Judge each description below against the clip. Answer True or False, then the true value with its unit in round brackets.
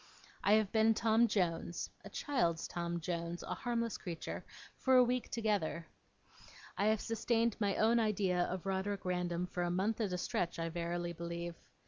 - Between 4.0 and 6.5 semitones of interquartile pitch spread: True (4.3 semitones)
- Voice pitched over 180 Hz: True (190 Hz)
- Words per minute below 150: False (170 wpm)